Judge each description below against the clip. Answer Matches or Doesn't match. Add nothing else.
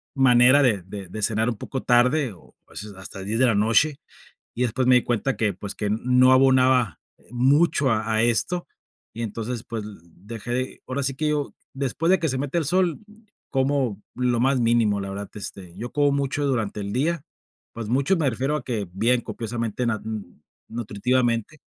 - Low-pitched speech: Matches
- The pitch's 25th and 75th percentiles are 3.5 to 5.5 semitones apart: Matches